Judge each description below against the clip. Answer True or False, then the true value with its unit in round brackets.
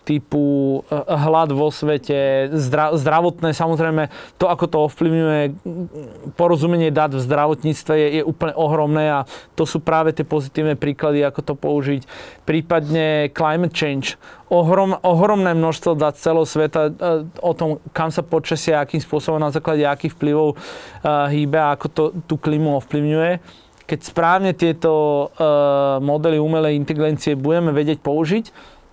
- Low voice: False (155 Hz)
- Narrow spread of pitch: True (1.6 semitones)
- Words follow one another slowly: False (135 wpm)